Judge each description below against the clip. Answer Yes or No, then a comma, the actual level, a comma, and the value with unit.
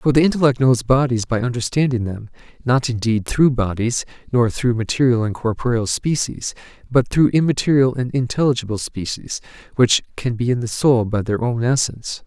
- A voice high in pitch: No, low, 125 Hz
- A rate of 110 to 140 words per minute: No, average, 165 wpm